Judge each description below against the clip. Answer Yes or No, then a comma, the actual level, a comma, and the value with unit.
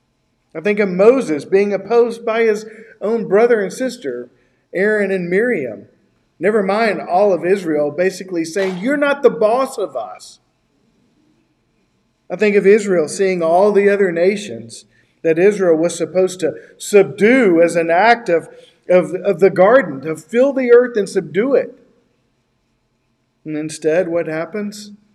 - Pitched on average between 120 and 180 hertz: No, high, 195 Hz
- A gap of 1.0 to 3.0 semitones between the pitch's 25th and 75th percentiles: No, average, 4.7 semitones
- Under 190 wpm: Yes, average, 150 wpm